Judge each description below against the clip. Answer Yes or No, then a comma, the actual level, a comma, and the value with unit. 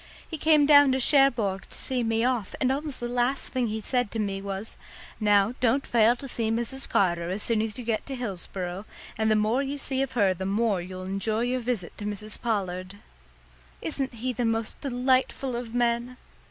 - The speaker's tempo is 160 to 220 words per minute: Yes, fast, 205 wpm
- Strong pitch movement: No, average, 3.9 semitones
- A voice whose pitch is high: Yes, high, 230 Hz